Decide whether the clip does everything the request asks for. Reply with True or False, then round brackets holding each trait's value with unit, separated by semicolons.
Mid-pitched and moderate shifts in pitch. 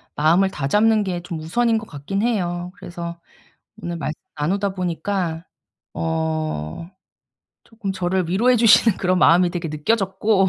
True (180 Hz; 3.6 semitones)